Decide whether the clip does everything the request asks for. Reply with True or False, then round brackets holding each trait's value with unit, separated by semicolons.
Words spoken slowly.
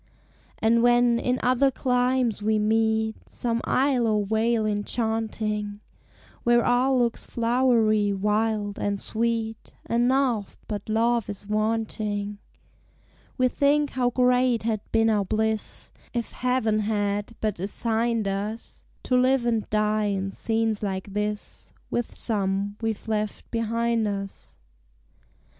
True (125 wpm)